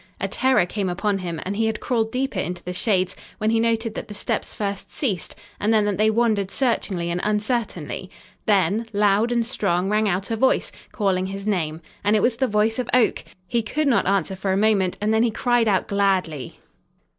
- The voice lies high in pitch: Yes, high, 210 Hz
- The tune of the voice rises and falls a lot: No, average, 3.0 semitones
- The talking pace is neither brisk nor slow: No, fast, 210 wpm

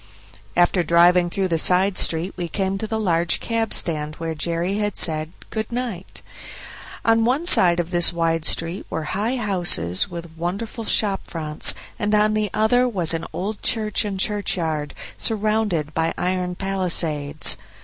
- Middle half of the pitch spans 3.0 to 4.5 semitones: Yes, average, 4.2 semitones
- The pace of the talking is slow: No, average, 160 wpm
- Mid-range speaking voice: Yes, medium, 180 Hz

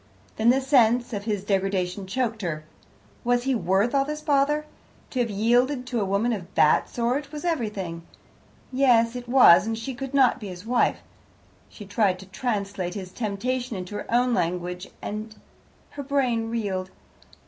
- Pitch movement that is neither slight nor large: Yes, average, 4.4 semitones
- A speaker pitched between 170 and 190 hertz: No, high, 225 Hz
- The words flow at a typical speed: Yes, average, 170 wpm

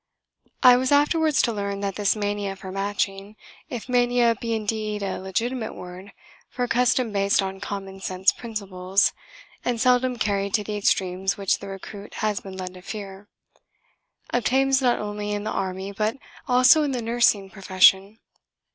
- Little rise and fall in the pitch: No, average, 3.7 semitones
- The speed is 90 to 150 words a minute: No, average, 165 wpm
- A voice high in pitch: Yes, high, 205 Hz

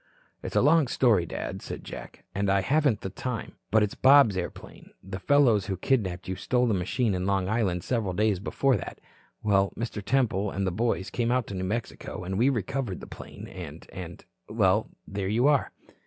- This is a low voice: Yes, low, 105 Hz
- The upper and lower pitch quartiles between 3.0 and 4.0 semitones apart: No, average, 4.7 semitones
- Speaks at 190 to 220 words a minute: Yes, average, 200 wpm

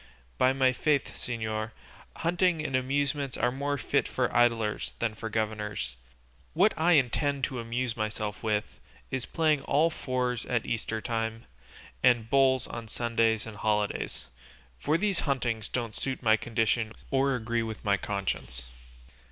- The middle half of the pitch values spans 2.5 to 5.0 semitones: Yes, average, 3.7 semitones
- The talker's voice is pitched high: No, low, 120 Hz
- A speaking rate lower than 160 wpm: Yes, average, 145 wpm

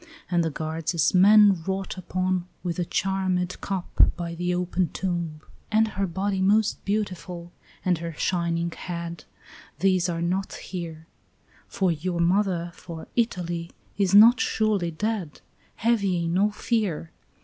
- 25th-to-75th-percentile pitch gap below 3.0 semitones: Yes, narrow, 2.4 semitones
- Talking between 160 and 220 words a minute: No, average, 140 wpm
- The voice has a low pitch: No, medium, 180 Hz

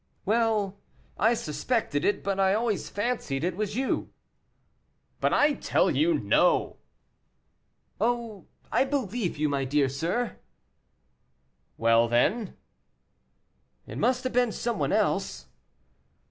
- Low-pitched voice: No, high, 210 Hz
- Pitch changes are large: Yes, wide, 7.9 semitones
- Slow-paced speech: Yes, slow, 120 wpm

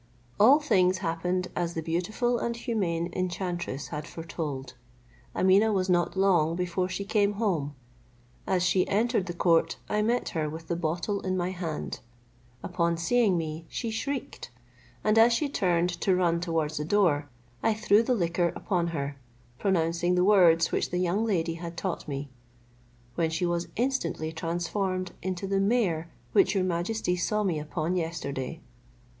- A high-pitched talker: No, medium, 180 Hz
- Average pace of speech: Yes, average, 160 wpm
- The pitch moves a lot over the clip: No, average, 3.2 semitones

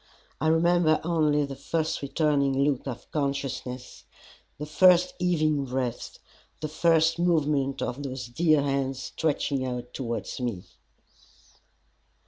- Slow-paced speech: Yes, slow, 115 wpm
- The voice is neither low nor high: Yes, medium, 145 Hz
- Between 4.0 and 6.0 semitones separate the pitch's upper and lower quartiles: No, average, 3.2 semitones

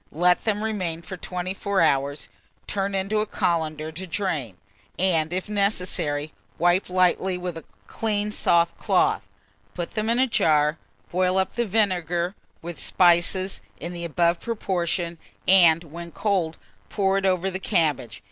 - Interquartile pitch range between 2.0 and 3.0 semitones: Yes, narrow, 2.6 semitones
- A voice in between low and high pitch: Yes, medium, 180 Hz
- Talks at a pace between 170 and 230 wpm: No, average, 145 wpm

